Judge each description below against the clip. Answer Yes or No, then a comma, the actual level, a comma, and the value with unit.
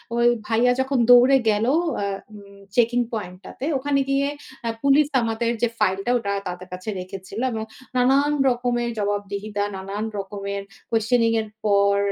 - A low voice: No, high, 220 Hz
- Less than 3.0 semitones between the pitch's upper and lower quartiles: No, average, 3.6 semitones